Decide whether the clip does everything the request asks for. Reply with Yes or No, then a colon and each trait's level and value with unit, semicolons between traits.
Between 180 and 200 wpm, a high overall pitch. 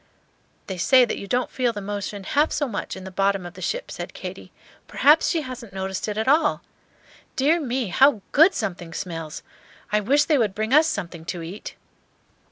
Yes: average, 195 wpm; high, 215 Hz